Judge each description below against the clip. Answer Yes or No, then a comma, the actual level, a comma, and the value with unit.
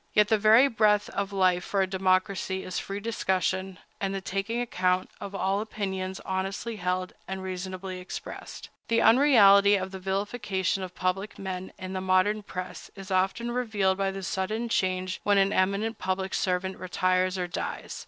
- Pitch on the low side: No, high, 190 Hz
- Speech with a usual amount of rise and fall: No, narrow, 1.6 semitones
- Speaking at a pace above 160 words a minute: Yes, average, 170 wpm